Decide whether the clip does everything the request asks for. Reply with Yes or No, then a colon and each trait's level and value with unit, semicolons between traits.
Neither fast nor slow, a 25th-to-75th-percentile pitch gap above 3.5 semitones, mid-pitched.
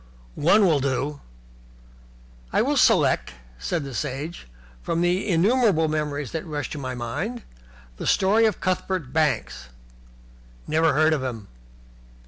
No: slow, 130 wpm; average, 4.8 semitones; medium, 155 Hz